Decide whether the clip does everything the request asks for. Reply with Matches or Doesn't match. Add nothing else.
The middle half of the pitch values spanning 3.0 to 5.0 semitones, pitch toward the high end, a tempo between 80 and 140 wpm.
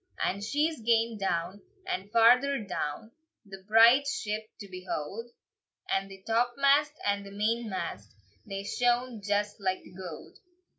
Matches